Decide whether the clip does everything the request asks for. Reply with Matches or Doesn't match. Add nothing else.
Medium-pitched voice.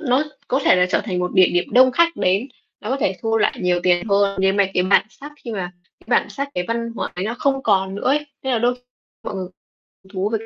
Doesn't match